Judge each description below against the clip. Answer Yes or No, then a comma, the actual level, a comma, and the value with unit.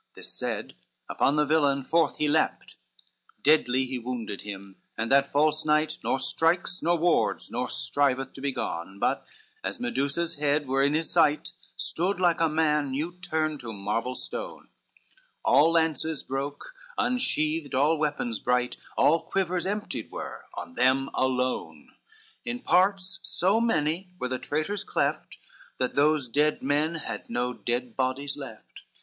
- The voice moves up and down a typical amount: Yes, average, 4.1 semitones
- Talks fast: No, average, 155 wpm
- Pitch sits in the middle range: Yes, medium, 145 Hz